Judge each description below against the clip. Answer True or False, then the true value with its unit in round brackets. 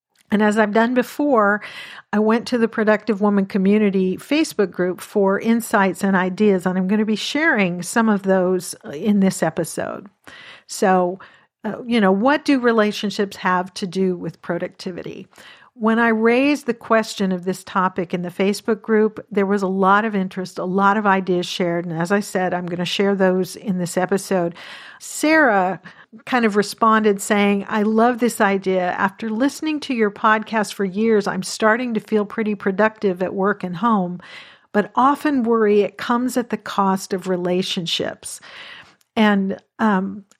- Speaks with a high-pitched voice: True (205 Hz)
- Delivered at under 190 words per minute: True (170 wpm)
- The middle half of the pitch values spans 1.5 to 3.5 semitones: True (3.0 semitones)